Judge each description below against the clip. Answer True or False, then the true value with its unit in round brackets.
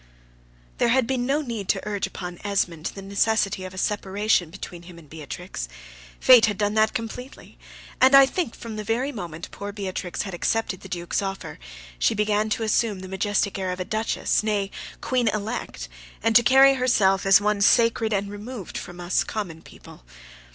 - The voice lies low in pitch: False (205 Hz)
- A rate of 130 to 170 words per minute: False (185 wpm)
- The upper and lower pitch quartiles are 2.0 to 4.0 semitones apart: True (3.3 semitones)